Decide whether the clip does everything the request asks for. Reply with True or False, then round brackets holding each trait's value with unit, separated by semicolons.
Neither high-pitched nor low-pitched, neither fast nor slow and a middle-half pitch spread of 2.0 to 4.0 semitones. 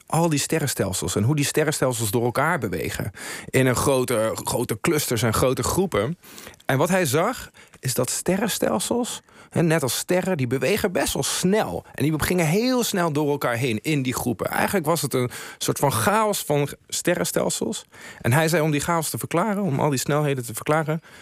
False (150 Hz; 190 wpm; 4.7 semitones)